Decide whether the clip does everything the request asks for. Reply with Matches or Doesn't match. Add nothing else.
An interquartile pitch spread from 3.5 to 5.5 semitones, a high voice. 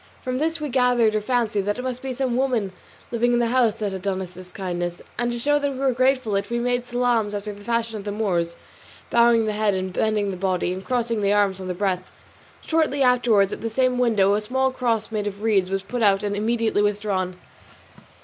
Matches